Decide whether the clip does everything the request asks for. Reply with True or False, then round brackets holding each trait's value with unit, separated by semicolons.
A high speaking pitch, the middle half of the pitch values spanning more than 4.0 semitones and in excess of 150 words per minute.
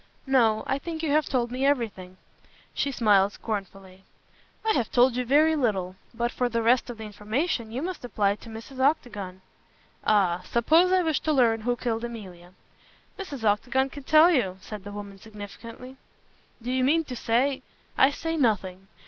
True (235 Hz; 4.8 semitones; 180 wpm)